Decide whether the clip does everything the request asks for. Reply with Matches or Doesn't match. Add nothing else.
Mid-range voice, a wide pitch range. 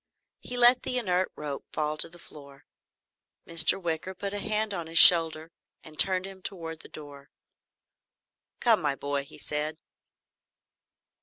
Doesn't match